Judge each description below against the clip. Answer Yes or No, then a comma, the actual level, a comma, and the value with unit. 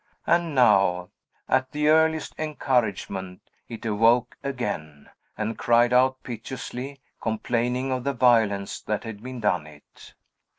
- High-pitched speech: No, low, 120 Hz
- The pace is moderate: No, slow, 125 wpm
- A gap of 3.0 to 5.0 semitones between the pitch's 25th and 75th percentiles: Yes, average, 3.9 semitones